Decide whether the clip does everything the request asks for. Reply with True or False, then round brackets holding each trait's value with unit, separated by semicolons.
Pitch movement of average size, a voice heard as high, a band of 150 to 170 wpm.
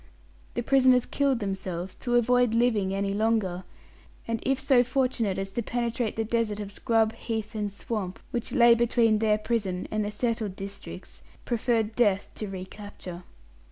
True (3.1 semitones; 220 Hz; 155 wpm)